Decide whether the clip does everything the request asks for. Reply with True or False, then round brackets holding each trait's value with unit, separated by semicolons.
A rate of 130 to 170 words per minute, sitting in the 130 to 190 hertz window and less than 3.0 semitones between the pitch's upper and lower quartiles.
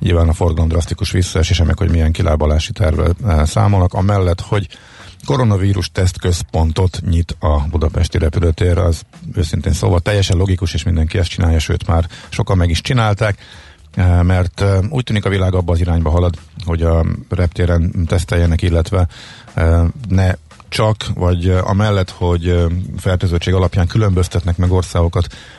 False (135 wpm; 90 Hz; 2.5 semitones)